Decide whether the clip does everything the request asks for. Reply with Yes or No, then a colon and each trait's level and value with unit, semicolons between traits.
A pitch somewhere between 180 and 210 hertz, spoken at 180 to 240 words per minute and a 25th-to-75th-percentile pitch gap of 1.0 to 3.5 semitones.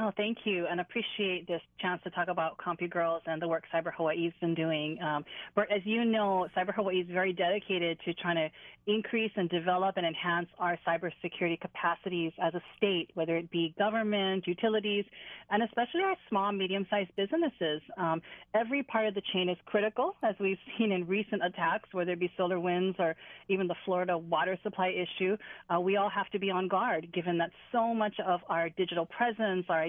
Yes: medium, 185 Hz; average, 195 wpm; average, 3.2 semitones